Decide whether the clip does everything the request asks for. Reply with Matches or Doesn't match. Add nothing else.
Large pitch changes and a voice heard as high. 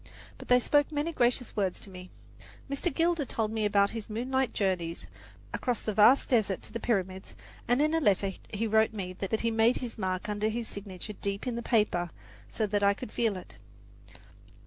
Doesn't match